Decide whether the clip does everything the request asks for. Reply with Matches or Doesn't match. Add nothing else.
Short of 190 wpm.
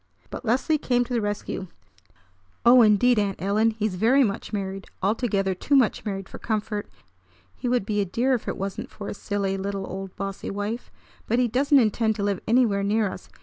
Doesn't match